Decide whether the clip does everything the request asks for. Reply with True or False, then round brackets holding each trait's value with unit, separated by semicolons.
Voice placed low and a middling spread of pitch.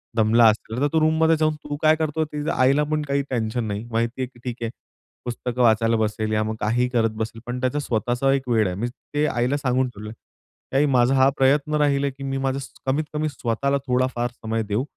True (125 Hz; 3.7 semitones)